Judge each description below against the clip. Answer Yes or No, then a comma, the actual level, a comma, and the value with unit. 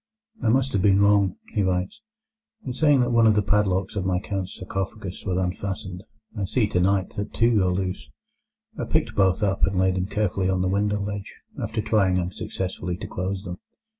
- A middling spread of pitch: No, narrow, 2.0 semitones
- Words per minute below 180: No, average, 195 wpm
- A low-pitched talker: Yes, very low, 95 Hz